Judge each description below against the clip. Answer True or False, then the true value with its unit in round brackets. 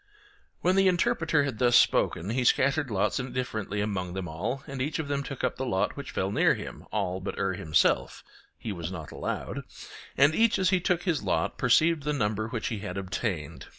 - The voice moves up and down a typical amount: False (7.3 semitones)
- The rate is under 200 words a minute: False (205 wpm)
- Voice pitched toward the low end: True (120 Hz)